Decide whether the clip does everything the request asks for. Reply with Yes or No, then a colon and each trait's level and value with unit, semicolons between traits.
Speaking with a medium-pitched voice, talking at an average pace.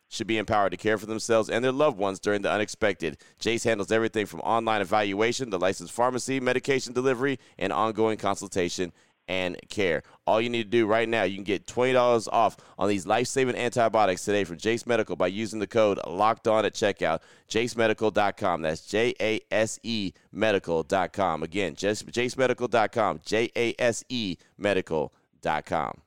No: low, 110 Hz; average, 150 wpm